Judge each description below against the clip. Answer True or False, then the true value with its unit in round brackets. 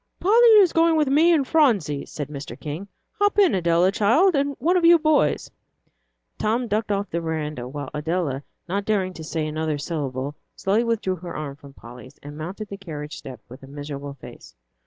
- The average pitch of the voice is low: False (175 Hz)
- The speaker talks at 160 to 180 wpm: False (190 wpm)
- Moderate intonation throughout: False (8.3 semitones)